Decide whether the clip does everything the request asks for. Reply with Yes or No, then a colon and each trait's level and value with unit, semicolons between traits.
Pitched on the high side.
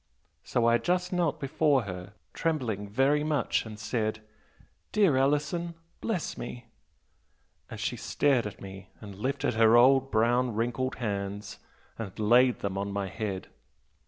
No: low, 120 Hz